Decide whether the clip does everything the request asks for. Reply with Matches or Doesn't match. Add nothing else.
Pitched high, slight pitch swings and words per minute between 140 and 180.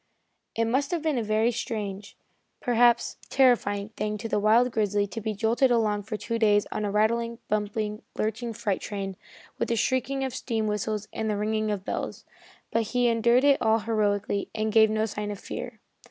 Doesn't match